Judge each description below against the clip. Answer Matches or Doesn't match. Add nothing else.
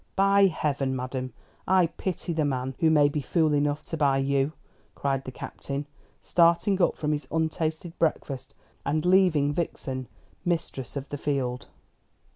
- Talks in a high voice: Doesn't match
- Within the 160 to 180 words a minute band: Doesn't match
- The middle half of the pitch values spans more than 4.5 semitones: Doesn't match